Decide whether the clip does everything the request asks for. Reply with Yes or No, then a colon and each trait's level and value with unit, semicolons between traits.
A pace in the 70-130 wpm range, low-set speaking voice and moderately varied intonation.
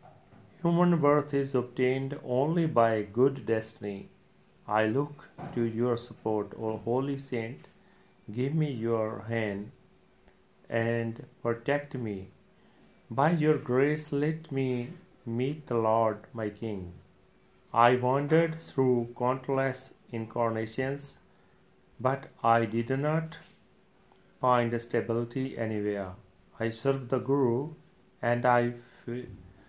Yes: average, 105 wpm; low, 125 Hz; average, 3.6 semitones